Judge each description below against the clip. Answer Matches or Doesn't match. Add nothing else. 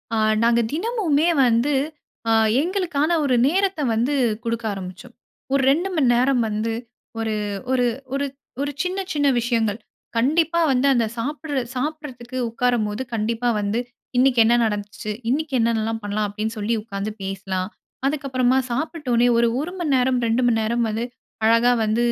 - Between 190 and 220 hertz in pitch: Doesn't match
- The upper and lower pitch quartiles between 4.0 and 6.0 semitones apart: Matches